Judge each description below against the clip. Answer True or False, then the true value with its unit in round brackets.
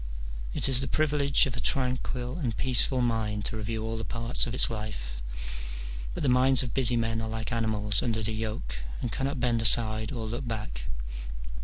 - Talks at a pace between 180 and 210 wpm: True (190 wpm)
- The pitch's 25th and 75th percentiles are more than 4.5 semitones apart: False (2.5 semitones)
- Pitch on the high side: False (115 Hz)